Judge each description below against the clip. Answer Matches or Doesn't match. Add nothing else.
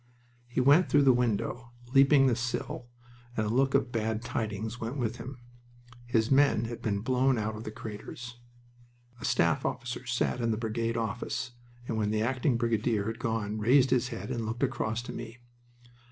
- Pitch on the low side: Matches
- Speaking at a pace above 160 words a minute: Matches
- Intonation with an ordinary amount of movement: Doesn't match